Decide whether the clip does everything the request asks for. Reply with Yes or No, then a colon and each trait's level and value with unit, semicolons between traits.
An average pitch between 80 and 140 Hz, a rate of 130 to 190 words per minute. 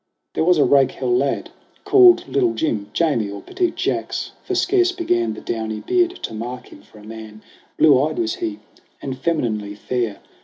Yes: low, 135 Hz; average, 180 wpm